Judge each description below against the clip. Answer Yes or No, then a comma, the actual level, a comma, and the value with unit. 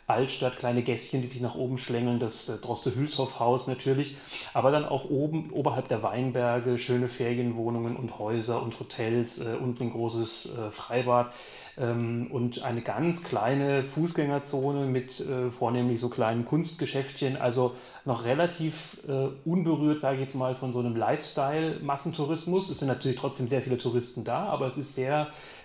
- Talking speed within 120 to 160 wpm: Yes, average, 155 wpm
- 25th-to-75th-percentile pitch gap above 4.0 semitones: No, narrow, 2.5 semitones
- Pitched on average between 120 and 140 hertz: Yes, low, 130 Hz